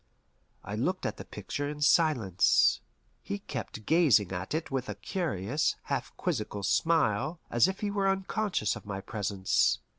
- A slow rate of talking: No, average, 155 wpm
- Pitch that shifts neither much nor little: No, wide, 8.7 semitones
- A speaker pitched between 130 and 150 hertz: Yes, low, 135 Hz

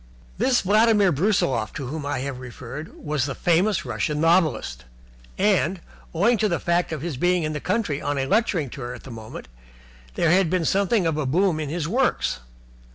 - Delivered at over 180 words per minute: Yes, average, 190 wpm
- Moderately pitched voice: Yes, medium, 165 Hz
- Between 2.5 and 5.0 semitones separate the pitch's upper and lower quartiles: No, wide, 5.4 semitones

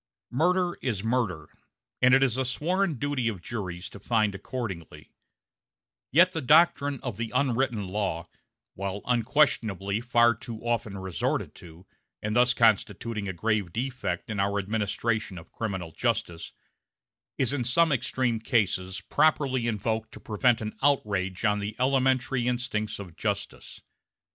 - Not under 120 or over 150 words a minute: Yes, average, 140 wpm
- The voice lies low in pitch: Yes, low, 115 Hz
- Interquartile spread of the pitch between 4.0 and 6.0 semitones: Yes, average, 4.3 semitones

